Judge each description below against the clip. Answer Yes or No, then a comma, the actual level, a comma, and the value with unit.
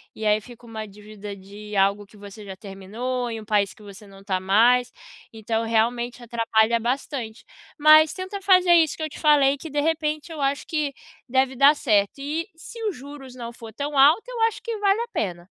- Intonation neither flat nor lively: No, wide, 6.1 semitones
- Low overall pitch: No, high, 245 Hz